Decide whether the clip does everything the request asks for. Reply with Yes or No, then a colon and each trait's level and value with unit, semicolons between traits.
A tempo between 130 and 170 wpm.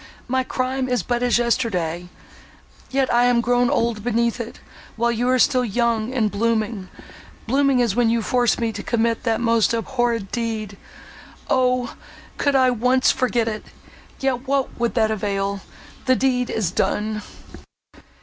Yes: average, 140 wpm